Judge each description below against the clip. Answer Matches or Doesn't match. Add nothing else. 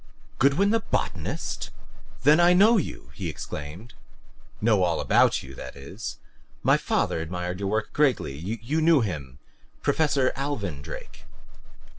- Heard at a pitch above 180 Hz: Doesn't match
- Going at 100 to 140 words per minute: Matches